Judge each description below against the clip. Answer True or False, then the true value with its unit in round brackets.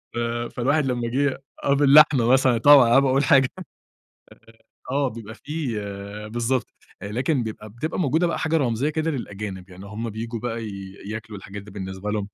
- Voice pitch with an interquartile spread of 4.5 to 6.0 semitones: True (4.8 semitones)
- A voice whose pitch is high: False (120 Hz)